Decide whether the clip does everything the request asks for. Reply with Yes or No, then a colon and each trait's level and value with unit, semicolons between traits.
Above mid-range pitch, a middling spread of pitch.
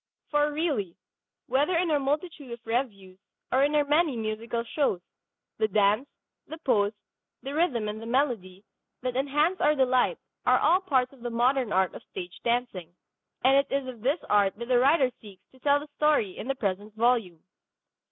Yes: very high, 250 Hz; average, 5.0 semitones